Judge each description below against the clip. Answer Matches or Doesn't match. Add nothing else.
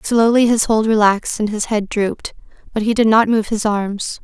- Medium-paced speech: Doesn't match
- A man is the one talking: Doesn't match